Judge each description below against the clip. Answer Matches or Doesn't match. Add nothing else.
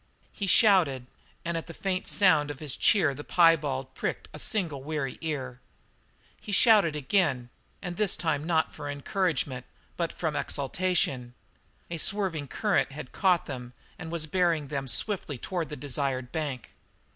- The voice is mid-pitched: Matches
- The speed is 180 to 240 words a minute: Doesn't match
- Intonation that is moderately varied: Matches